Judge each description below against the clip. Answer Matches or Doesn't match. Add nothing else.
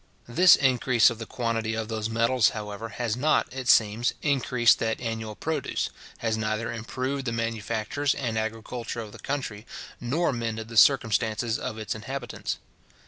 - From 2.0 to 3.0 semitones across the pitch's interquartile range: Matches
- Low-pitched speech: Matches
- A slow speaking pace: Doesn't match